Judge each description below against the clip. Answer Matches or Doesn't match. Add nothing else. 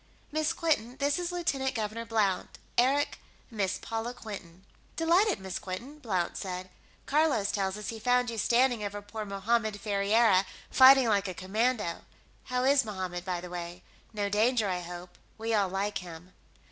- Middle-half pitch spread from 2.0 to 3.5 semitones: Doesn't match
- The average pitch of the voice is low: Doesn't match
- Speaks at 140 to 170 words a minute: Matches